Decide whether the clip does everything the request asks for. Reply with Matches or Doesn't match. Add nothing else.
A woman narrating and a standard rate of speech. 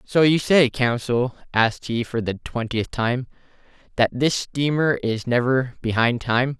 Doesn't match